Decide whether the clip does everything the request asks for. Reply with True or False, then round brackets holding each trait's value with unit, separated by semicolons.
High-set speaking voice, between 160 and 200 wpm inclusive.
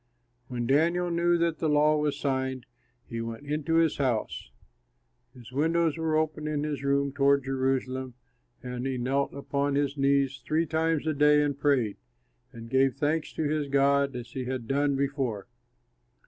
False (140 Hz; 165 wpm)